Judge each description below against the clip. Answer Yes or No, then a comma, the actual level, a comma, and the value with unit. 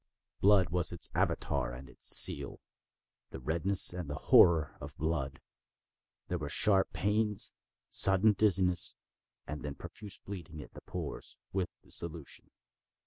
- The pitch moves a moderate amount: Yes, average, 4.3 semitones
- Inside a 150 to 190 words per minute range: No, slow, 135 wpm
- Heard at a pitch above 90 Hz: No, very low, 85 Hz